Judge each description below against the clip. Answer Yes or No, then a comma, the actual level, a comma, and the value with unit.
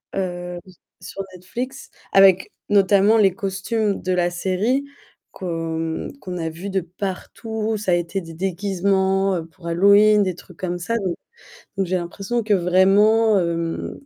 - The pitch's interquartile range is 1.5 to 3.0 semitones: Yes, narrow, 2.4 semitones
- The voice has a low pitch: No, high, 190 Hz